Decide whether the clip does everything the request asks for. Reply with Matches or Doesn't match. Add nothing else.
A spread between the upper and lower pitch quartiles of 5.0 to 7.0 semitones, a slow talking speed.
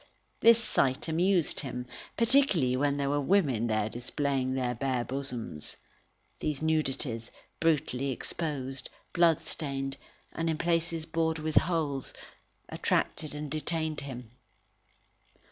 Doesn't match